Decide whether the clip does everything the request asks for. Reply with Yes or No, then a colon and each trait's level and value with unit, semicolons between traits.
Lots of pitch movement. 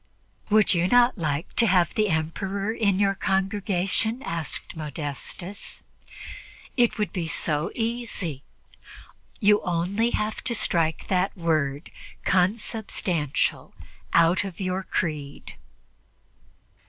No: average, 4.2 semitones